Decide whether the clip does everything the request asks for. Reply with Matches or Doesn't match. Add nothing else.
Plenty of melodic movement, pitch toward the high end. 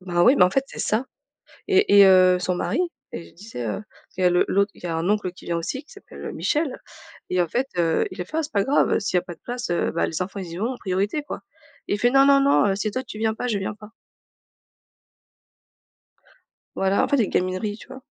Matches